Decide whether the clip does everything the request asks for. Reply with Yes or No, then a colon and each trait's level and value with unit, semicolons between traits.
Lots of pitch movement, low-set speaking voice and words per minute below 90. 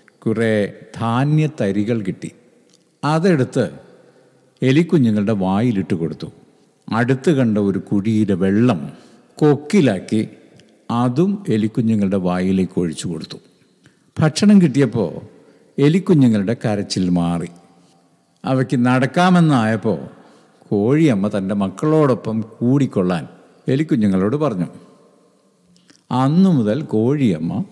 Yes: wide, 6.2 semitones; low, 115 Hz; average, 75 wpm